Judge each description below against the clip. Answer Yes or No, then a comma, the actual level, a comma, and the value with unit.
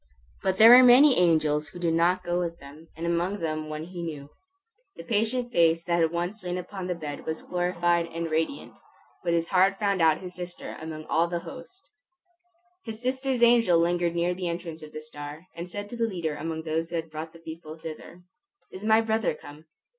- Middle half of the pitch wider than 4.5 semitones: No, average, 2.8 semitones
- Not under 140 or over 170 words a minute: No, fast, 205 wpm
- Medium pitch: Yes, medium, 170 Hz